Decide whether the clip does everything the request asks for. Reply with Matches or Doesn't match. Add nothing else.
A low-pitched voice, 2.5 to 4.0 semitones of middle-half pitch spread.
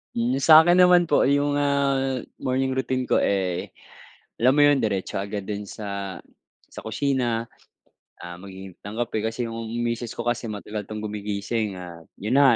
Doesn't match